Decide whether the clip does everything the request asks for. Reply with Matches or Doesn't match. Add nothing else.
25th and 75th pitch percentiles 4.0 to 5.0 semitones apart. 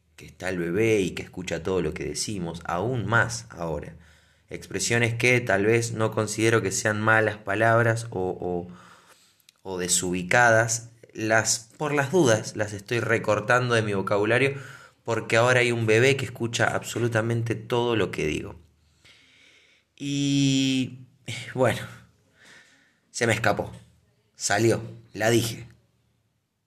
Doesn't match